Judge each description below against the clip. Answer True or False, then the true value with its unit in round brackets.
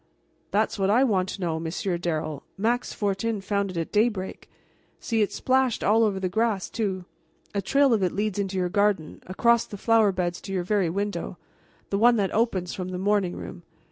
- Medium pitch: False (200 Hz)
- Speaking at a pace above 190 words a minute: True (200 wpm)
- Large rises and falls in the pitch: False (3.0 semitones)